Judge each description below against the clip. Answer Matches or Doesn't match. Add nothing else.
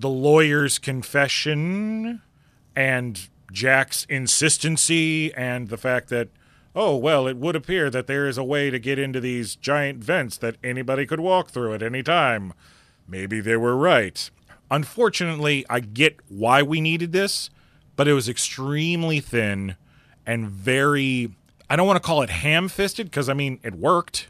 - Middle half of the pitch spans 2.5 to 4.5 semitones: Matches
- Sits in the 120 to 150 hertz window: Matches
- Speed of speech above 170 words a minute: Doesn't match